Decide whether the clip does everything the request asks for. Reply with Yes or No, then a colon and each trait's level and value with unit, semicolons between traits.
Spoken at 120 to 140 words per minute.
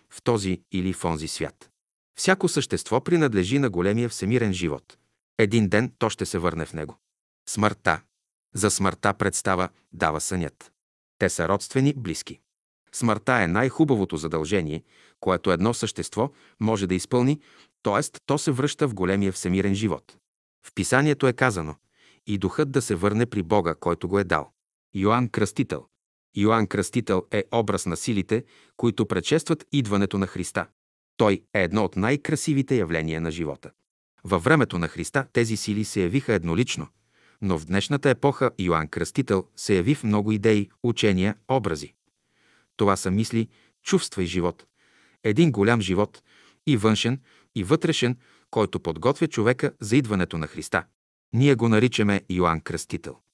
No: average, 150 wpm